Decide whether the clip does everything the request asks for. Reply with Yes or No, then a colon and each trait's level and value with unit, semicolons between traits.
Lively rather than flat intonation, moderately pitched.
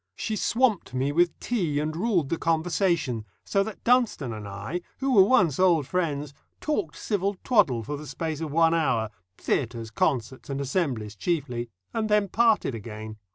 Yes: wide, 7.2 semitones; medium, 160 Hz